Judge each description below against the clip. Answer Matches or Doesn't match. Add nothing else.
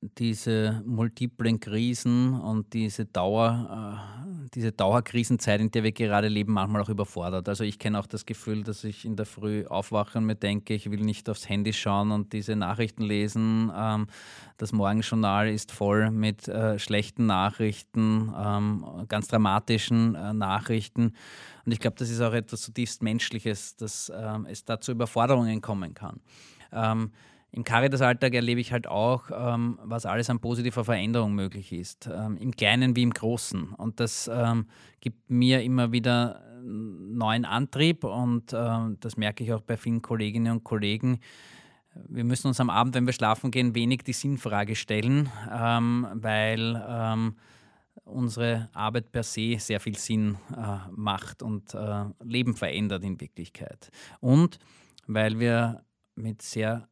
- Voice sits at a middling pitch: Doesn't match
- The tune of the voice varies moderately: Doesn't match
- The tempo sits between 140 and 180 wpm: Matches